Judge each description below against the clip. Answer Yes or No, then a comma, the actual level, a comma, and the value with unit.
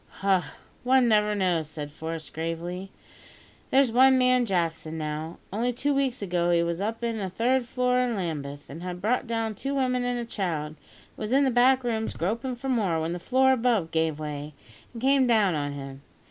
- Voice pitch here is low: No, high, 210 Hz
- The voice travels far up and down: Yes, wide, 7.2 semitones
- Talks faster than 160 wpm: Yes, average, 200 wpm